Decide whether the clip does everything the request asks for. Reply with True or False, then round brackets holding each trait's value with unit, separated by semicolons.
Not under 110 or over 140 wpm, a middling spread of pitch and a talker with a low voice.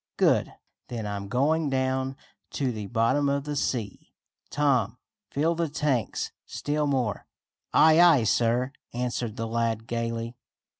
True (135 wpm; 3.9 semitones; 125 Hz)